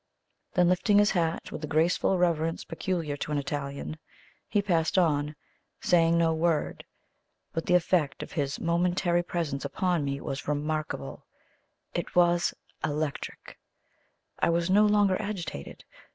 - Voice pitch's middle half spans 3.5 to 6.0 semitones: No, average, 3.1 semitones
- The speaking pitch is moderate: Yes, medium, 165 Hz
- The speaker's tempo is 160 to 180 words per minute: No, slow, 135 wpm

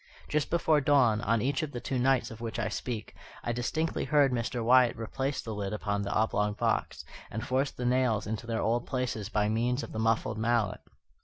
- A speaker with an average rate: No, fast, 210 wpm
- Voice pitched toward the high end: No, low, 120 Hz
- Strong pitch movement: No, average, 2.9 semitones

